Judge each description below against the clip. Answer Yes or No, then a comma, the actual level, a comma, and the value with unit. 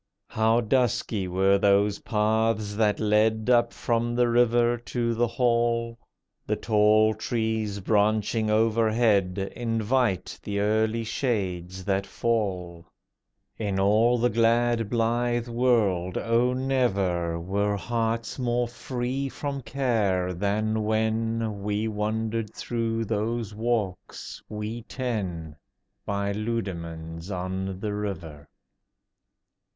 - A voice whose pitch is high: No, low, 110 Hz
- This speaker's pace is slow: Yes, slow, 105 wpm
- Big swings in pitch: No, narrow, 2.6 semitones